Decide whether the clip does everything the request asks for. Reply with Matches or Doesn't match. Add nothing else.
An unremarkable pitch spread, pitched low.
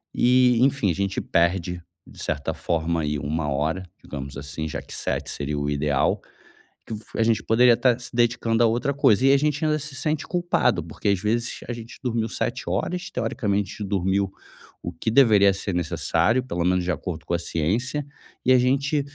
Doesn't match